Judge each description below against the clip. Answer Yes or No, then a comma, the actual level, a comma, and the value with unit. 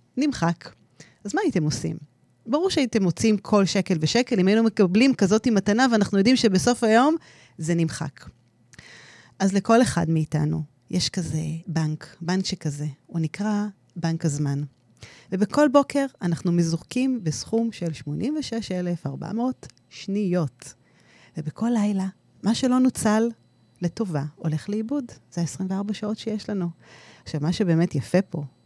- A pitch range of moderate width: No, wide, 6.0 semitones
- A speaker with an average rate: Yes, average, 130 wpm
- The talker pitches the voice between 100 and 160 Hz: No, medium, 185 Hz